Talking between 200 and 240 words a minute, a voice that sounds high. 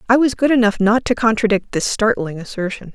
Yes: fast, 205 wpm; high, 220 Hz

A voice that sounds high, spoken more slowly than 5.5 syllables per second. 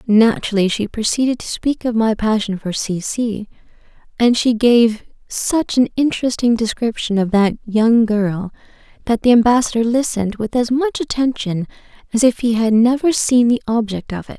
Yes: high, 230 Hz; 5.0 syllables/s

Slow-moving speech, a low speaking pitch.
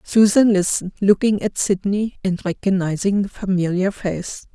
No: slow, 130 wpm; high, 195 Hz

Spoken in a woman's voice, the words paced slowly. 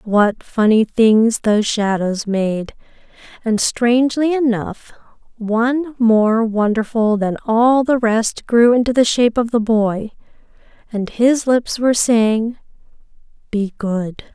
Yes: female; slow, 125 wpm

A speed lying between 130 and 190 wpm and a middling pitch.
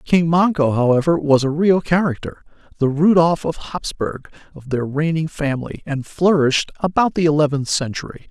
Yes: average, 150 wpm; medium, 155 Hz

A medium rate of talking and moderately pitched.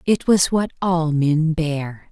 Yes: average, 170 wpm; medium, 160 Hz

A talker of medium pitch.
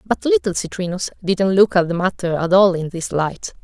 Yes: medium, 180 Hz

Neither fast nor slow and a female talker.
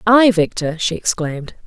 Yes: average, 145 wpm; female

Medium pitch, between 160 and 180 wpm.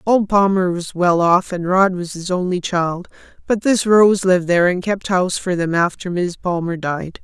No: medium, 180 Hz; fast, 205 wpm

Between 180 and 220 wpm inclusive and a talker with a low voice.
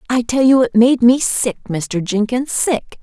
No: average, 200 wpm; high, 240 Hz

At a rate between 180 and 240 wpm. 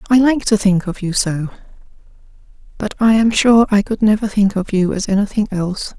Yes: average, 200 wpm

